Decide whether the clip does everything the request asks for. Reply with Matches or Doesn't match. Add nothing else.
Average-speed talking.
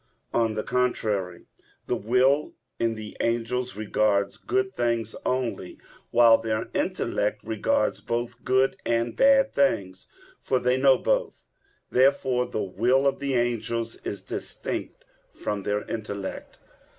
Doesn't match